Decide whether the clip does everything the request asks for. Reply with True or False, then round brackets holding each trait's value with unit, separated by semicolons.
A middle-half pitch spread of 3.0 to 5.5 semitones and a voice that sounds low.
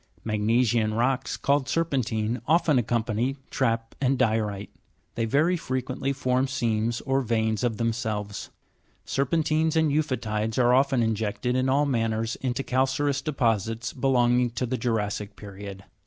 True (3.3 semitones; 120 Hz)